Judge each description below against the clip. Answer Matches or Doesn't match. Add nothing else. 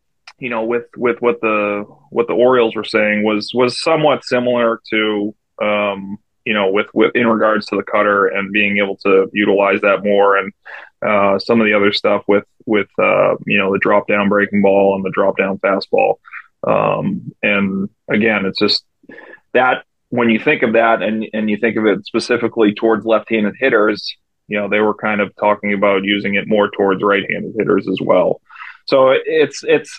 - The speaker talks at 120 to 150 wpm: Doesn't match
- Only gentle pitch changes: Matches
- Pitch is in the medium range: Doesn't match